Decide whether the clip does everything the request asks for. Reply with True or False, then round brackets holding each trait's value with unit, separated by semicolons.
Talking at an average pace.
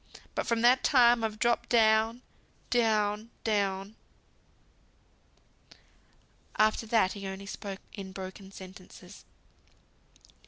False (95 wpm)